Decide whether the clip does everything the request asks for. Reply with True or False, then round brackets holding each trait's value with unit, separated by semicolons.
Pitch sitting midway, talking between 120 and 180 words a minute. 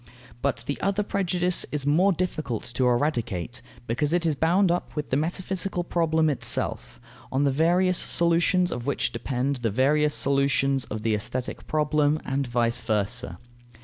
True (145 Hz; 155 wpm)